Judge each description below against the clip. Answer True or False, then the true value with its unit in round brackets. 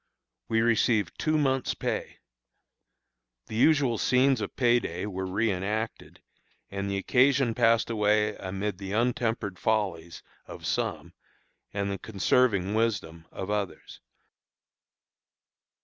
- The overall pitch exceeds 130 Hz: False (105 Hz)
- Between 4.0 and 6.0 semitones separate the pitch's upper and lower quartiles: False (3.3 semitones)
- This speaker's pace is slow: True (115 wpm)